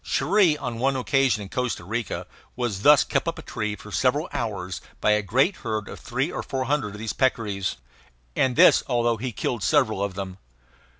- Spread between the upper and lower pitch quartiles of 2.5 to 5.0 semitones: Yes, average, 4.3 semitones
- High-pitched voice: No, low, 120 Hz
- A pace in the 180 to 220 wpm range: Yes, average, 195 wpm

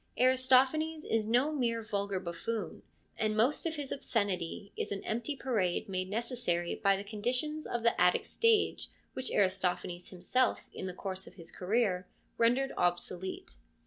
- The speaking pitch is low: No, high, 220 Hz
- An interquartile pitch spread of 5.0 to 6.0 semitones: Yes, wide, 5.4 semitones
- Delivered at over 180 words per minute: No, average, 155 wpm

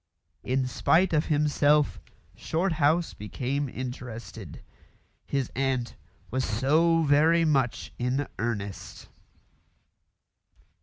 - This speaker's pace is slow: Yes, slow, 85 wpm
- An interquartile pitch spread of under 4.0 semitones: Yes, average, 3.6 semitones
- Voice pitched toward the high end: No, medium, 140 Hz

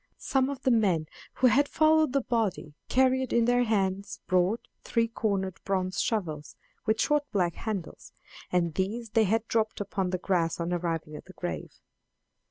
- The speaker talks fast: No, average, 170 wpm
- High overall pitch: Yes, high, 210 Hz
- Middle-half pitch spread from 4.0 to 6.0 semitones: Yes, average, 4.9 semitones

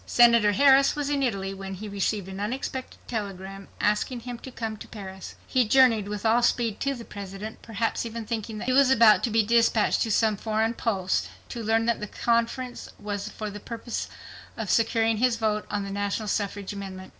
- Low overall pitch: No, high, 220 Hz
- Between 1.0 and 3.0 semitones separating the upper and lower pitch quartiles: Yes, narrow, 2.5 semitones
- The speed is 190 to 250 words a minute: Yes, average, 200 wpm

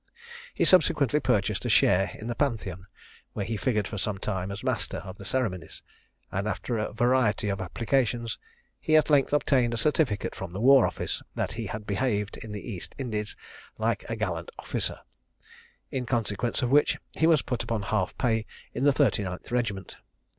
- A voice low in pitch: Yes, low, 110 Hz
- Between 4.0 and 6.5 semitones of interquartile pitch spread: Yes, average, 4.4 semitones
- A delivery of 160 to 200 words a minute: Yes, average, 180 wpm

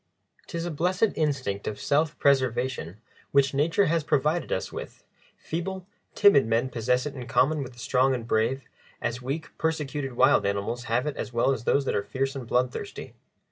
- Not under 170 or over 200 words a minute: Yes, average, 180 wpm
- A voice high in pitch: No, low, 135 Hz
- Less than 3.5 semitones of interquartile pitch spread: No, average, 3.9 semitones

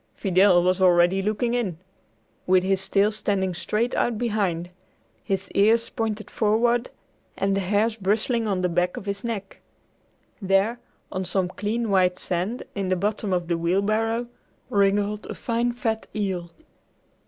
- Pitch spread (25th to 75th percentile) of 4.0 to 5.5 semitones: No, average, 3.1 semitones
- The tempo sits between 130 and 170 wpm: Yes, average, 150 wpm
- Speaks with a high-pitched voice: Yes, high, 200 Hz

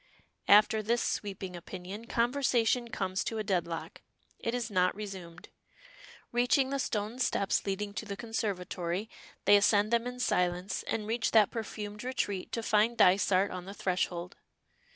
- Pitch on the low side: No, high, 205 Hz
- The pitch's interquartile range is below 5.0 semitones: Yes, average, 3.6 semitones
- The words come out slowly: No, average, 150 wpm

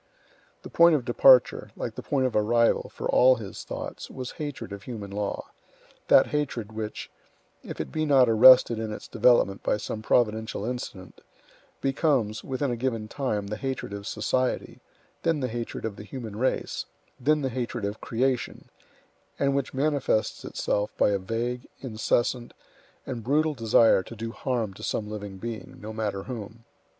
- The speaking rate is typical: Yes, average, 165 wpm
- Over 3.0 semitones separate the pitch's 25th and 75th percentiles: Yes, average, 3.4 semitones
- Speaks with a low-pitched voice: Yes, low, 115 Hz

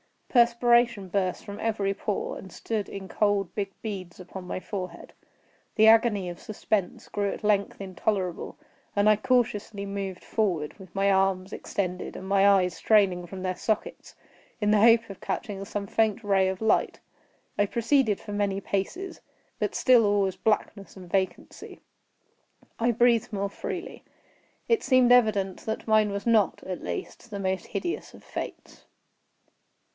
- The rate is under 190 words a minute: Yes, average, 155 wpm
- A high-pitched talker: Yes, high, 200 Hz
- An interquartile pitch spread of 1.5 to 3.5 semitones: Yes, narrow, 2.5 semitones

